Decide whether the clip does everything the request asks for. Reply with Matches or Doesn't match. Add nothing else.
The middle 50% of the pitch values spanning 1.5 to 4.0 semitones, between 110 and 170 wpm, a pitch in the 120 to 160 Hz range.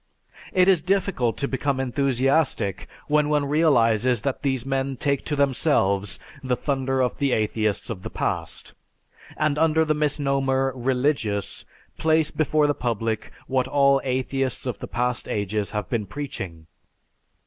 Matches